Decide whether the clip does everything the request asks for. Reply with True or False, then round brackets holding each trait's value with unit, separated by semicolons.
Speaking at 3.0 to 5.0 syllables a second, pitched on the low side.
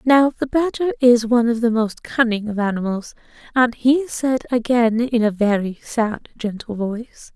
False (4.6 syllables/s; 235 Hz)